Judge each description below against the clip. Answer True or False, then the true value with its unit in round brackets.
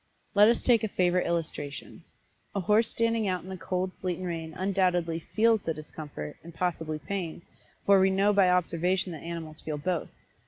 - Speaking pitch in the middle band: True (180 Hz)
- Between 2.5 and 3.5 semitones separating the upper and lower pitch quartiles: True (3.2 semitones)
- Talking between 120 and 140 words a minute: False (185 wpm)